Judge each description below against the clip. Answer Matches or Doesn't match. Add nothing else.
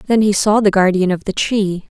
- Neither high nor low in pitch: Doesn't match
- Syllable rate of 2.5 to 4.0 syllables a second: Doesn't match